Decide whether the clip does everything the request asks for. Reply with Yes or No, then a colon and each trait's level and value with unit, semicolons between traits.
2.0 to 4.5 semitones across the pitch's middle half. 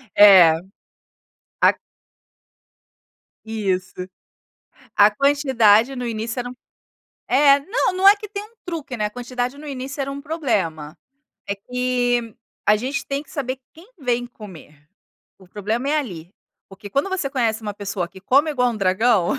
No: average, 5.3 semitones